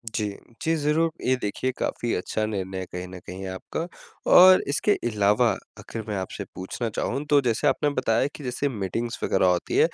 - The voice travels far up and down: Yes, wide, 6.8 semitones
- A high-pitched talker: No, low, 115 Hz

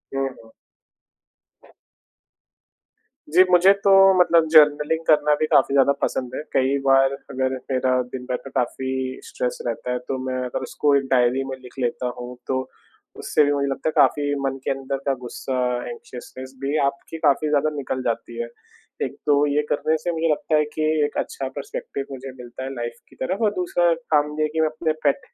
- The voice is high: No, low, 135 Hz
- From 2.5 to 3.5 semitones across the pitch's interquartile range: Yes, average, 2.8 semitones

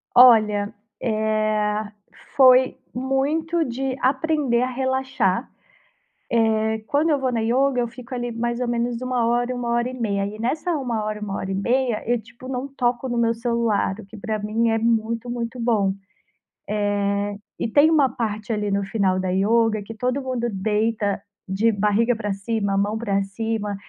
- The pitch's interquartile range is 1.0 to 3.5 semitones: Yes, average, 3.0 semitones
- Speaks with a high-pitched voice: Yes, high, 230 Hz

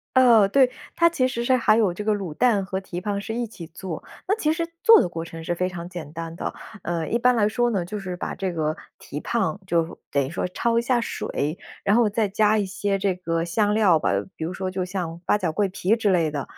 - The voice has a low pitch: No, high, 195 Hz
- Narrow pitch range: No, average, 4.6 semitones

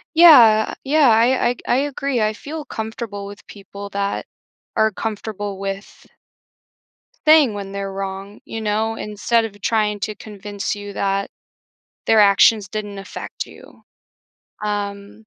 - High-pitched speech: Yes, high, 210 Hz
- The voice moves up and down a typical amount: No, narrow, 2.0 semitones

